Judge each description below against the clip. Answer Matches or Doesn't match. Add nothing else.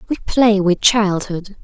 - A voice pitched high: Matches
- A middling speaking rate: Matches